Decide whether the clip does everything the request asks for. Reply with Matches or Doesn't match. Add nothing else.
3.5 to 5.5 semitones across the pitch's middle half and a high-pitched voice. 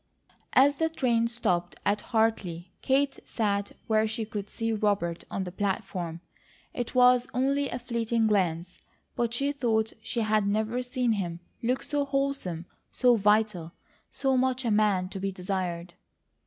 Matches